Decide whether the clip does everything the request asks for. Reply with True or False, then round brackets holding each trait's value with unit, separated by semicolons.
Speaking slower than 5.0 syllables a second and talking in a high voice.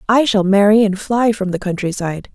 False (5.1 syllables/s; 205 Hz)